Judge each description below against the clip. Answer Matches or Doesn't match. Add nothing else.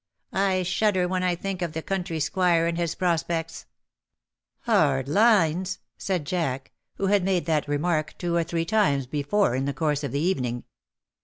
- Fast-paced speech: Doesn't match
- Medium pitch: Matches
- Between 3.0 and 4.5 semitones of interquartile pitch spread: Matches